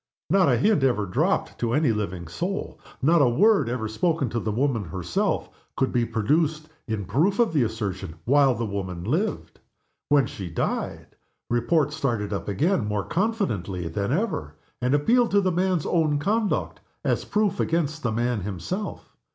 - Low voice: Yes, low, 130 Hz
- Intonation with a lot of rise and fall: Yes, wide, 8.2 semitones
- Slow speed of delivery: No, average, 165 wpm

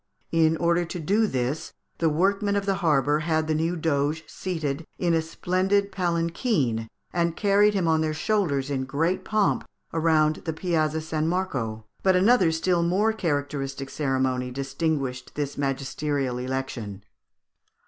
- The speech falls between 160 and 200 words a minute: No, average, 145 wpm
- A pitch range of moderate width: Yes, average, 4.5 semitones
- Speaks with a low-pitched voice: No, medium, 160 Hz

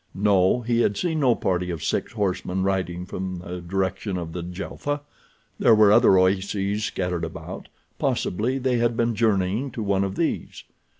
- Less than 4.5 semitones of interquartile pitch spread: Yes, average, 3.9 semitones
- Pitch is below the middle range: Yes, low, 100 Hz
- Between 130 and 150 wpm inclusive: No, average, 160 wpm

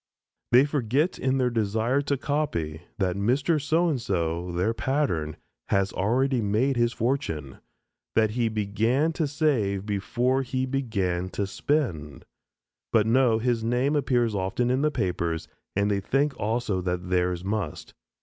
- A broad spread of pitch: Yes, wide, 5.7 semitones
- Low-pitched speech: Yes, low, 115 Hz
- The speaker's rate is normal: Yes, average, 150 wpm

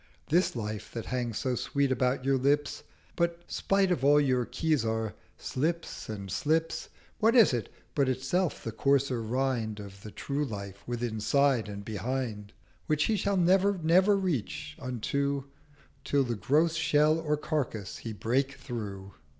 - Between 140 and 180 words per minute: Yes, average, 150 wpm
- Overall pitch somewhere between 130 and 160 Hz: Yes, low, 135 Hz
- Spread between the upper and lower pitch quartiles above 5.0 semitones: Yes, wide, 5.5 semitones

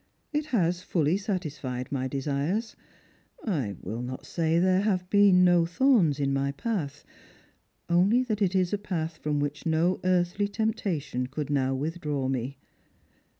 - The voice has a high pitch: No, medium, 170 Hz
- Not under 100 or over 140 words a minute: No, average, 150 wpm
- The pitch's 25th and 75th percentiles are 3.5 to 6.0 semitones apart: Yes, wide, 5.5 semitones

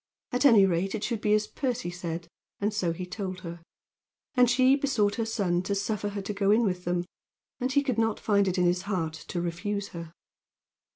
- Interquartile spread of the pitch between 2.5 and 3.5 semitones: No, average, 3.9 semitones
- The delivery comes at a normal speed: No, fast, 215 wpm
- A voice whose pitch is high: Yes, high, 200 Hz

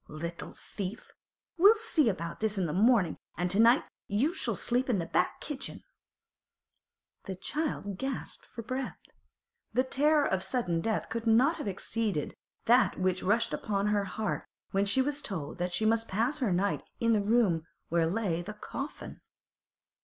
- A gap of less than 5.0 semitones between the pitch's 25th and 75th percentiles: No, average, 5.3 semitones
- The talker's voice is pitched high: Yes, high, 215 Hz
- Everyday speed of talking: Yes, average, 170 wpm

